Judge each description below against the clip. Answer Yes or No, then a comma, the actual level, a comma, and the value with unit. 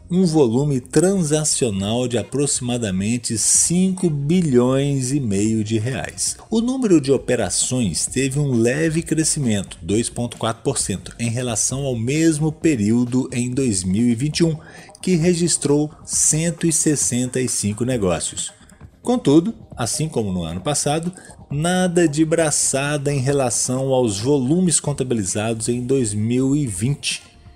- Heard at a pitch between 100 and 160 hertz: Yes, low, 135 Hz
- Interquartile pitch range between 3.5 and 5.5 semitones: Yes, average, 5.0 semitones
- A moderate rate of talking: No, slow, 100 wpm